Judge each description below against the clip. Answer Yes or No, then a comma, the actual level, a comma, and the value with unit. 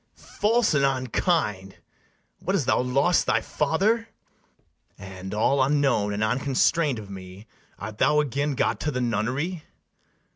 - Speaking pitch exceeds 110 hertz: Yes, low, 135 Hz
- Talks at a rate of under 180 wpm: Yes, slow, 135 wpm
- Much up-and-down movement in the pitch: Yes, wide, 6.0 semitones